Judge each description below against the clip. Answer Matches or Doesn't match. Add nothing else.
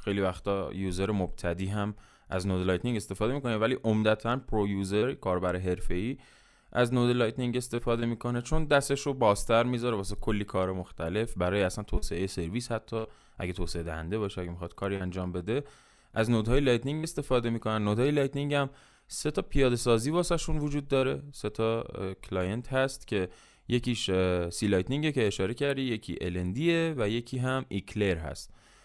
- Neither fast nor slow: Doesn't match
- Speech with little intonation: Doesn't match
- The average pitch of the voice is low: Matches